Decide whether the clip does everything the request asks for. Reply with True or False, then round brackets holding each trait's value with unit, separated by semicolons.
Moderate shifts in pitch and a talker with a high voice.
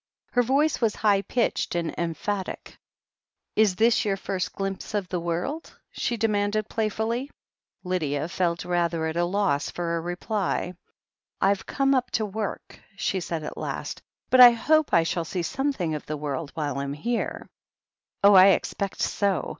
True (4.6 semitones; 195 Hz)